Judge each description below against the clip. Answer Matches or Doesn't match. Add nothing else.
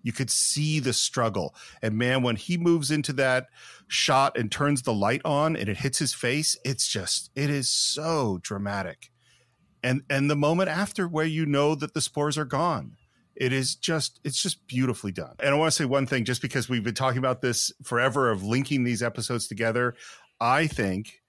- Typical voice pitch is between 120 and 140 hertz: Matches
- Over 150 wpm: Matches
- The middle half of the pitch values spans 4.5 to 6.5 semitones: Doesn't match